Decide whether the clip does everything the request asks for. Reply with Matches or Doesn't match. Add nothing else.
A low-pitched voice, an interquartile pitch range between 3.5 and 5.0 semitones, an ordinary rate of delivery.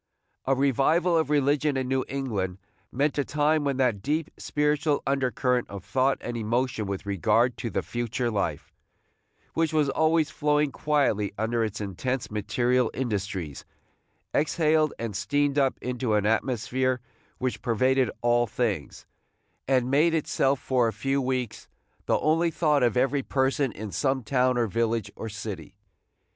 Matches